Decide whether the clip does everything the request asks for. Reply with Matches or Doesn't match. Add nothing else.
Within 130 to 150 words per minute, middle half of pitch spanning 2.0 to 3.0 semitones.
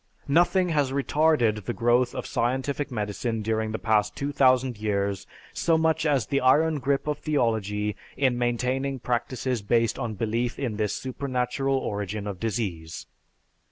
Doesn't match